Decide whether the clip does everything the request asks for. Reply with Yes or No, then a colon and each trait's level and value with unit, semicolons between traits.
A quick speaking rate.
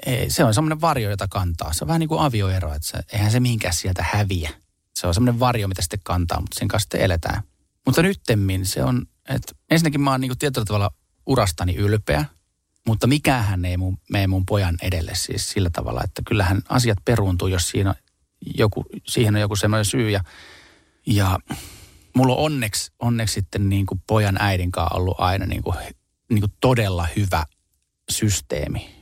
Yes: fast, 185 wpm